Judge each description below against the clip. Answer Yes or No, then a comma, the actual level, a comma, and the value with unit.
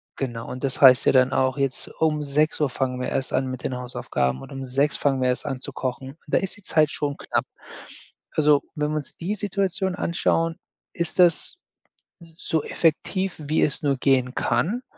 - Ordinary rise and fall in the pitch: Yes, average, 3.8 semitones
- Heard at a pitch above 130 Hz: Yes, medium, 140 Hz